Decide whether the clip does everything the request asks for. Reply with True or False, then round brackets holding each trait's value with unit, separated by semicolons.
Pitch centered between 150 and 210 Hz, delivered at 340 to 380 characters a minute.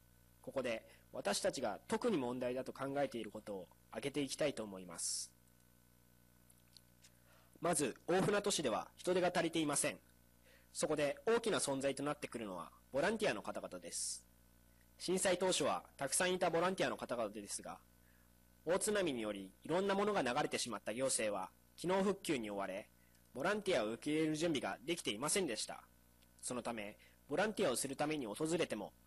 False (110 Hz; 365 characters per minute)